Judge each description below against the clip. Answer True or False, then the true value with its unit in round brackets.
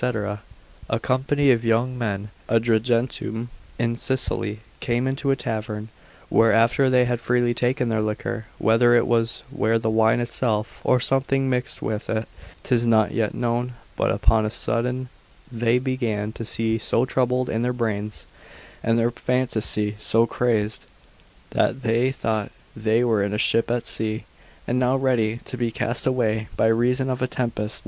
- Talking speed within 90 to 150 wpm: False (165 wpm)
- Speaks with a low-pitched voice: True (115 Hz)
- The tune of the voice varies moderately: False (2.1 semitones)